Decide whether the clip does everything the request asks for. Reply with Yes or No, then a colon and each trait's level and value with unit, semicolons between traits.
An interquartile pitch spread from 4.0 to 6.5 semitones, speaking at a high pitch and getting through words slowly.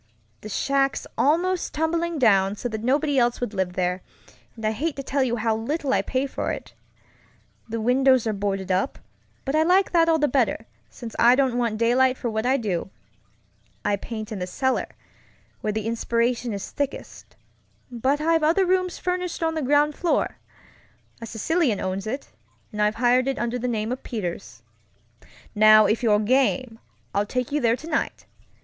No: average, 4.7 semitones; high, 245 Hz; average, 180 wpm